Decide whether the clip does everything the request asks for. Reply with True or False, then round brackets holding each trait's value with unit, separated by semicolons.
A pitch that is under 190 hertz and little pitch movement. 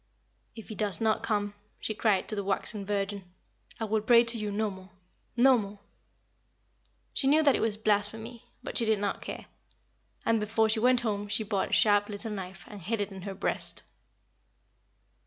False (210 Hz; 1.9 semitones)